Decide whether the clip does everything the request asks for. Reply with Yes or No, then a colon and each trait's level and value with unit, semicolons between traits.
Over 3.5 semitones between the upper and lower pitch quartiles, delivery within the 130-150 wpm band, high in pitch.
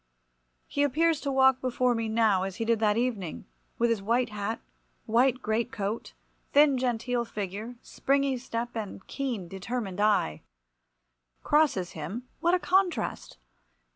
Yes: average, 4.1 semitones; average, 140 wpm; high, 235 Hz